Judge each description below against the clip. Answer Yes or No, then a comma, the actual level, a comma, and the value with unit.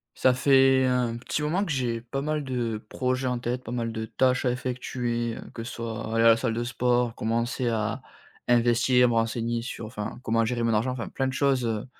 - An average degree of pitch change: No, narrow, 1.9 semitones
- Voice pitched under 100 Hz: No, low, 120 Hz